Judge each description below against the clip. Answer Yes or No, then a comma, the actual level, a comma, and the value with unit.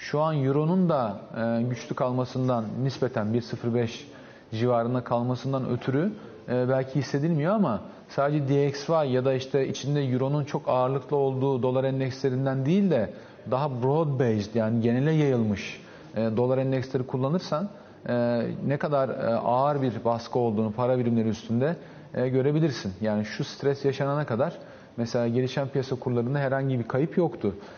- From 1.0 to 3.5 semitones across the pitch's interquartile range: Yes, average, 2.8 semitones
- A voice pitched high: No, low, 130 Hz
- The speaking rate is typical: Yes, average, 130 wpm